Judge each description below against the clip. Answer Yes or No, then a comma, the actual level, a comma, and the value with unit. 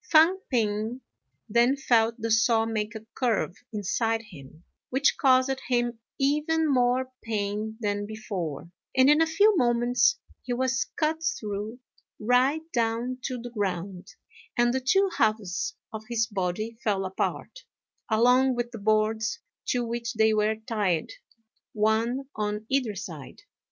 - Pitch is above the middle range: Yes, high, 230 Hz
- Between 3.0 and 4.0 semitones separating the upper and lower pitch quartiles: Yes, average, 3.3 semitones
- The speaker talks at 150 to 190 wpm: No, average, 140 wpm